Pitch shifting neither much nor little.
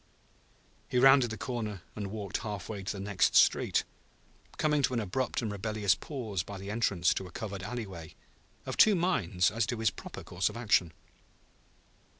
Yes: average, 3.6 semitones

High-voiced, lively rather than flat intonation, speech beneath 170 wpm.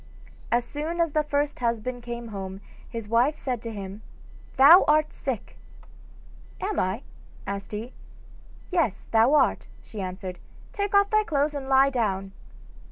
Yes: high, 245 Hz; wide, 6.1 semitones; average, 150 wpm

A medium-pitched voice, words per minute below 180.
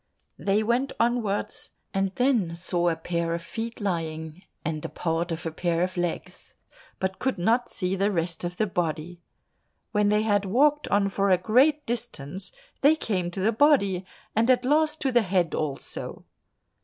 No: high, 195 Hz; average, 170 wpm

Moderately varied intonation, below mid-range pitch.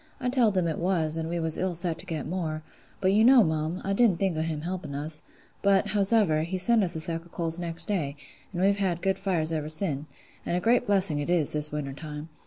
No: average, 3.6 semitones; medium, 170 Hz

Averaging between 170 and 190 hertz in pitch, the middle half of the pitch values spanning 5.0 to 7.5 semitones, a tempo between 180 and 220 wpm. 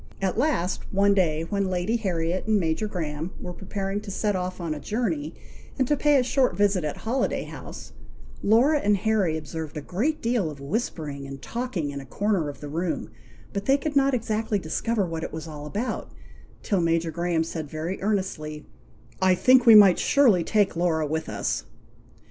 Yes: medium, 185 Hz; average, 5.3 semitones; average, 190 wpm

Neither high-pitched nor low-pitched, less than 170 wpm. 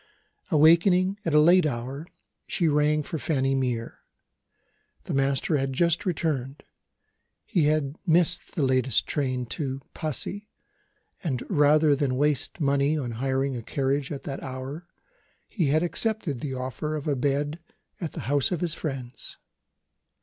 Yes: medium, 145 Hz; average, 150 wpm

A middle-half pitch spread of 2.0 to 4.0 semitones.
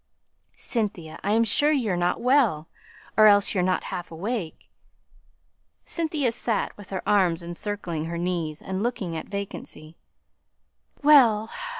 No: average, 5.0 semitones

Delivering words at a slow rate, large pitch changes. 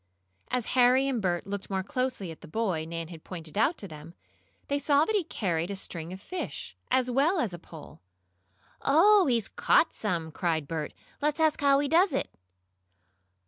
No: average, 185 wpm; wide, 8.8 semitones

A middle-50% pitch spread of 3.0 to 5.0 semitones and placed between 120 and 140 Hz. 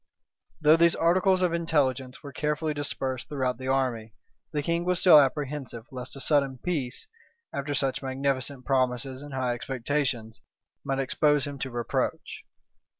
No: narrow, 2.5 semitones; low, 135 Hz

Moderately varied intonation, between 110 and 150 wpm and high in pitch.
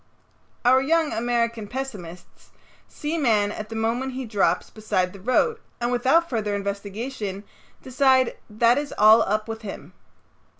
Yes: average, 3.9 semitones; average, 145 wpm; high, 230 Hz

